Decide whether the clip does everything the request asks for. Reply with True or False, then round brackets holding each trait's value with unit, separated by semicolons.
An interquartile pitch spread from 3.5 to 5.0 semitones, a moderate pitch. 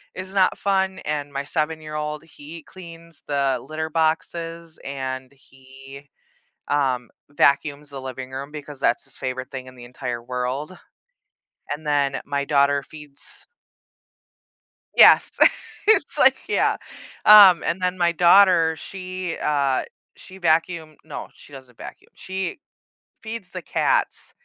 True (4.0 semitones; 150 Hz)